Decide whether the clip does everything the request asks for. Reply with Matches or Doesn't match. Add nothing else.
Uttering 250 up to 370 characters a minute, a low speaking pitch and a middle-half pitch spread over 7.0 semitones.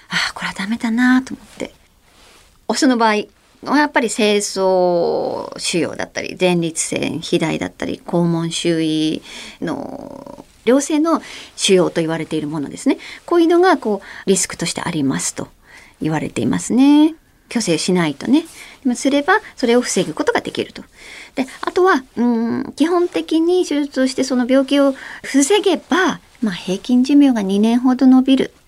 Doesn't match